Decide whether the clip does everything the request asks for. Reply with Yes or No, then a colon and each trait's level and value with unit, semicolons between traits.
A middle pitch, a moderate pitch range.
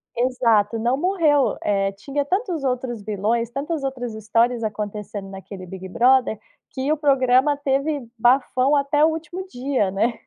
No: very high, 250 Hz; average, 4.7 semitones